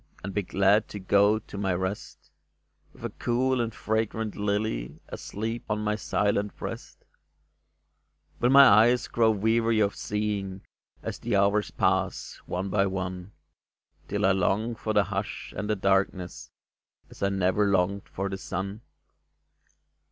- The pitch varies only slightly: Yes, narrow, 2.0 semitones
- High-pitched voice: No, low, 100 Hz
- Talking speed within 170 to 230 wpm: No, average, 145 wpm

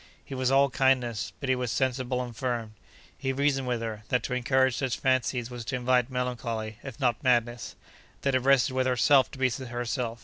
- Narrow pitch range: Yes, narrow, 1.7 semitones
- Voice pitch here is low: Yes, low, 125 Hz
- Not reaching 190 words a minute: No, average, 200 wpm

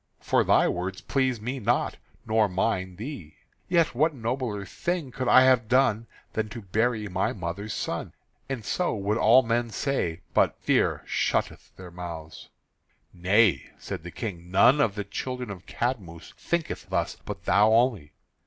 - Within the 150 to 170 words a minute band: Yes, average, 160 wpm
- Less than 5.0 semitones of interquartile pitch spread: No, average, 5.3 semitones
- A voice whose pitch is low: Yes, low, 110 Hz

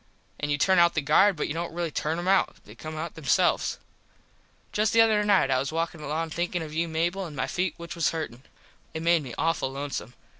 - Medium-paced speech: No, fast, 235 wpm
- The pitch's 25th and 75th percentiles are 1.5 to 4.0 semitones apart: Yes, narrow, 2.6 semitones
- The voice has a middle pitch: Yes, medium, 165 Hz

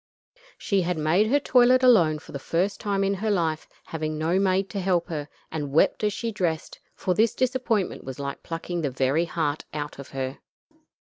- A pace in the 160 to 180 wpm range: No, average, 195 wpm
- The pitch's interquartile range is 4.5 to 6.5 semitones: Yes, average, 4.8 semitones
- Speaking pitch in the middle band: Yes, medium, 175 Hz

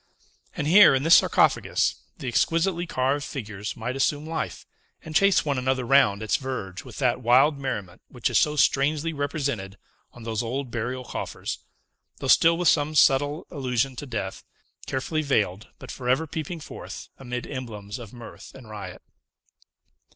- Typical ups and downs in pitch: Yes, average, 4.2 semitones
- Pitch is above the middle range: No, low, 130 Hz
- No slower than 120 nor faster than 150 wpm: No, average, 160 wpm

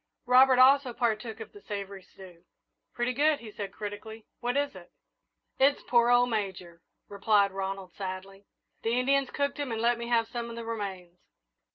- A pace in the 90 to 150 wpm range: No, average, 175 wpm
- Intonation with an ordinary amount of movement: Yes, average, 4.0 semitones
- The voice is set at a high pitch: Yes, high, 225 Hz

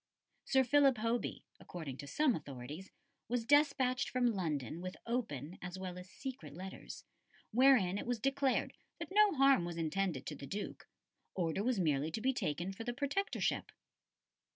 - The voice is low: No, high, 205 Hz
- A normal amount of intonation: No, wide, 7.6 semitones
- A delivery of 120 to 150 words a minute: No, average, 160 wpm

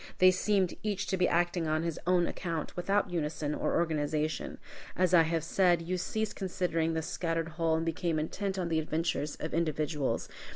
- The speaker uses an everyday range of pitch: No, narrow, 2.3 semitones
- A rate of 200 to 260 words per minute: No, average, 180 wpm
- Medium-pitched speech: Yes, medium, 165 Hz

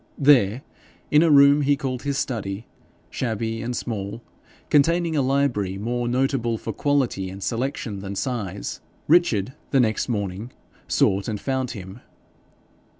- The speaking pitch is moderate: No, low, 120 Hz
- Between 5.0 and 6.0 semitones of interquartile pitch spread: Yes, average, 5.3 semitones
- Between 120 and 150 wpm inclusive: Yes, average, 140 wpm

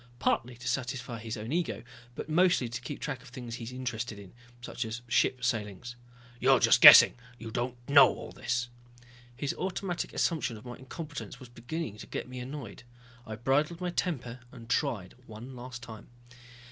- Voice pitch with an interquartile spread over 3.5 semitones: No, average, 3.0 semitones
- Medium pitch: No, low, 125 Hz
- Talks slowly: No, average, 185 wpm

